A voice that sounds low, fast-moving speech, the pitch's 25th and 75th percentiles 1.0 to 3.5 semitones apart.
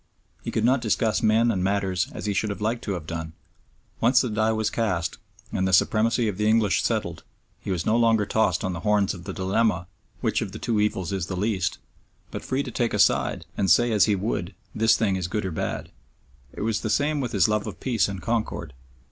Yes: low, 105 Hz; fast, 230 wpm; average, 3.2 semitones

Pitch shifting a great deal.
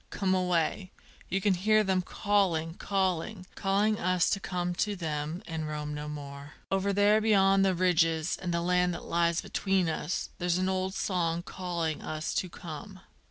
No: average, 2.8 semitones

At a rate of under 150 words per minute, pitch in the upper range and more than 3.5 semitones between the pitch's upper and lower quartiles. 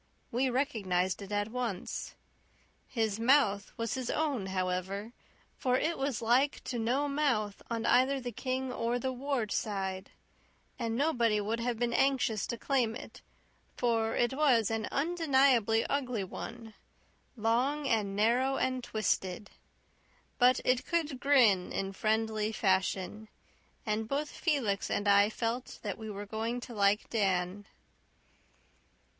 Yes: average, 140 wpm; high, 230 Hz; average, 4.0 semitones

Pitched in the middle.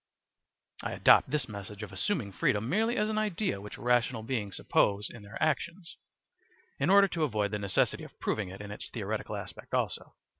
No: low, 115 Hz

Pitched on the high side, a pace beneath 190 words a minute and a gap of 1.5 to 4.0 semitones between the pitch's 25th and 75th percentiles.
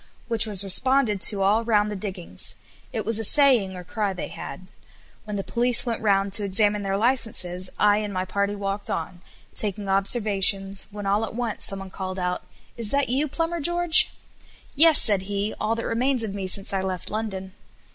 No: high, 205 Hz; average, 195 wpm; average, 2.9 semitones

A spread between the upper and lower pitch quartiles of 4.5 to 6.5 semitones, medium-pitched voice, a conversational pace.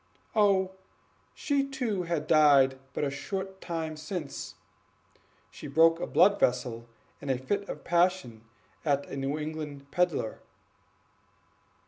No: average, 5.2 semitones; medium, 155 Hz; slow, 125 wpm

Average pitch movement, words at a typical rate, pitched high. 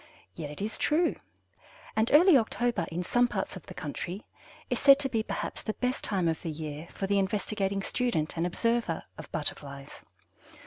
No: wide, 6.6 semitones; average, 180 wpm; high, 200 Hz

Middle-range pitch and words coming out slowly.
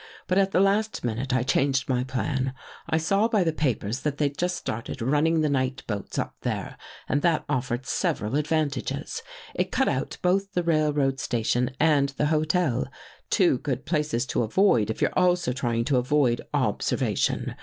No: medium, 145 Hz; average, 175 wpm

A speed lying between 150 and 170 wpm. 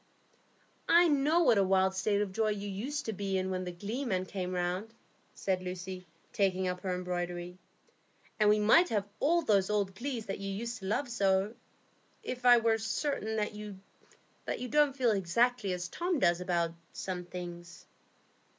No: average, 180 wpm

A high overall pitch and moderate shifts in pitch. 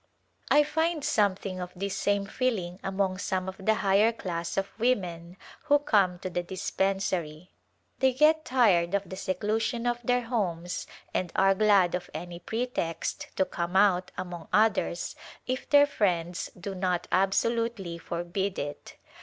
Yes: high, 195 Hz; average, 4.3 semitones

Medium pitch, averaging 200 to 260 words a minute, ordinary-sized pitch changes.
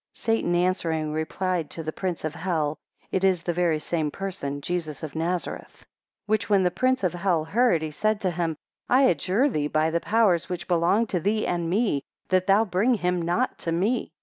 Yes: medium, 180 Hz; fast, 205 wpm; average, 3.6 semitones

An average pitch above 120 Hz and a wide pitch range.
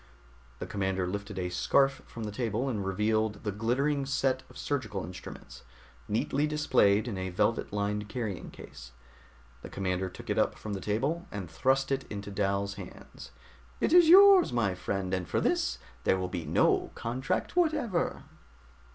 No: low, 105 Hz; wide, 5.8 semitones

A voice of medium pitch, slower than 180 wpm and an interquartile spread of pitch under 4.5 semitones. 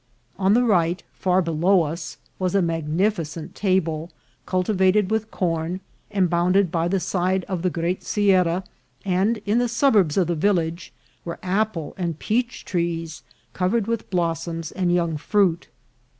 Yes: medium, 180 Hz; average, 150 wpm; average, 2.9 semitones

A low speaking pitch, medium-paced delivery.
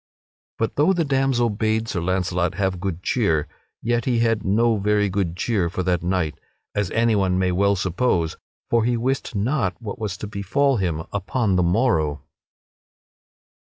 Yes: low, 100 Hz; average, 165 wpm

